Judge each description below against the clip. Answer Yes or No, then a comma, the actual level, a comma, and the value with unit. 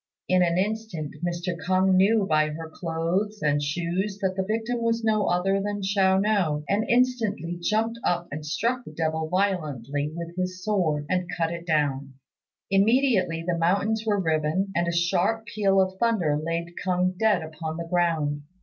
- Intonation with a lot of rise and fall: No, average, 3.8 semitones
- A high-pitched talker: No, medium, 180 Hz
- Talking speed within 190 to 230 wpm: No, average, 170 wpm